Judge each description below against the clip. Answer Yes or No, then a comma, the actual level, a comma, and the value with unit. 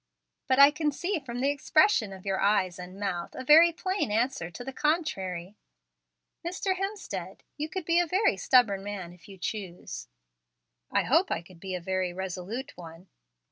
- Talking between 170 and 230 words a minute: Yes, average, 180 wpm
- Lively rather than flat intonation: Yes, wide, 8.7 semitones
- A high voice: Yes, high, 215 Hz